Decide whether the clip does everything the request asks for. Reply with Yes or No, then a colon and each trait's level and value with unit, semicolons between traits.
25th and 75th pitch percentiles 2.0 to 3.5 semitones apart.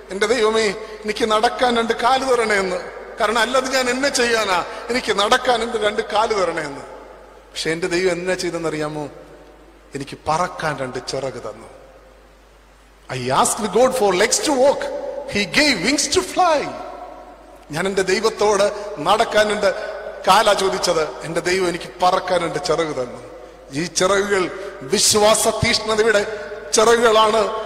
No: average, 4.6 semitones